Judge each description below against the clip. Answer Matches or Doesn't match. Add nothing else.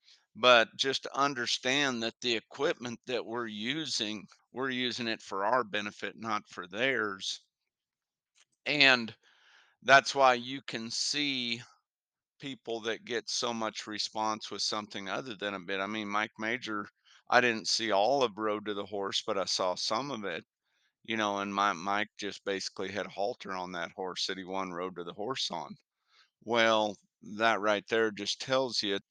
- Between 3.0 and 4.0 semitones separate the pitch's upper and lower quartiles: Matches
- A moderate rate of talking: Matches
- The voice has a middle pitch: Doesn't match